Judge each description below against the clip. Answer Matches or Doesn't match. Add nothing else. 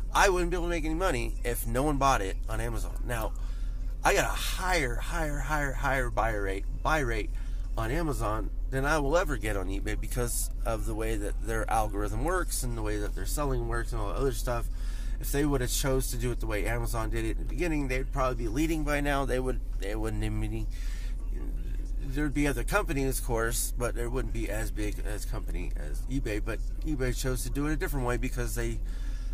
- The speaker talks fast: Matches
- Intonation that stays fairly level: Doesn't match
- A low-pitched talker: Matches